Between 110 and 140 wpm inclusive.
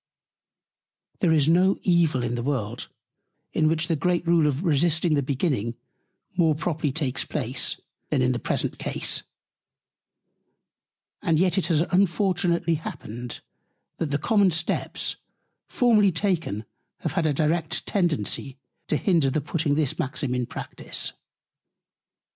Yes: slow, 135 wpm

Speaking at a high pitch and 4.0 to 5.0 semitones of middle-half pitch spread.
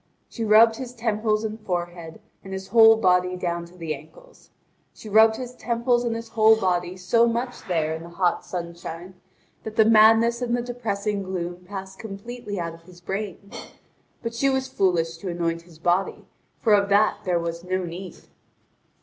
Yes: high, 200 Hz; average, 4.4 semitones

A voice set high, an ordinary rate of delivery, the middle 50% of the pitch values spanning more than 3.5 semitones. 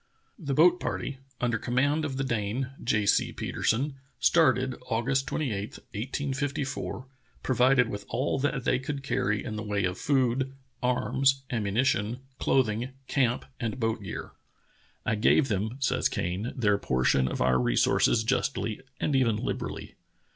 No: low, 125 Hz; average, 145 wpm; average, 4.1 semitones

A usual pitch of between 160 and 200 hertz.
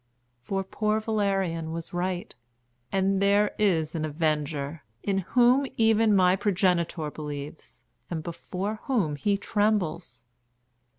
Yes: medium, 185 Hz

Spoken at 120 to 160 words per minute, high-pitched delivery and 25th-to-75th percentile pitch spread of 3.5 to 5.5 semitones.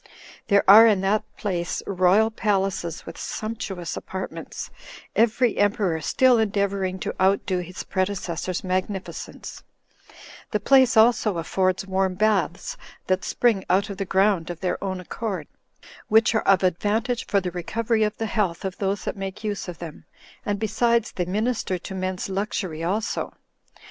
No: average, 150 wpm; high, 195 Hz; average, 2.7 semitones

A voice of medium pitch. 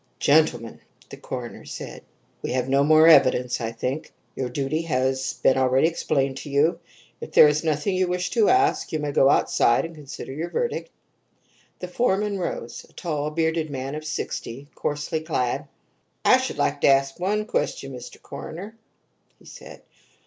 Yes: medium, 150 Hz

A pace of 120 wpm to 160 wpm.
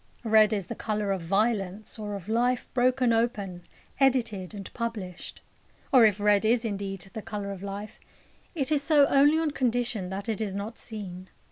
No: average, 175 wpm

